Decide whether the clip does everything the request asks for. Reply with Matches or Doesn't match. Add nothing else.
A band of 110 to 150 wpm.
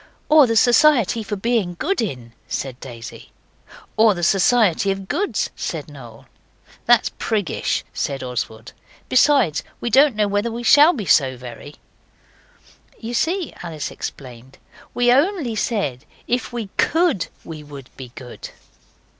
Matches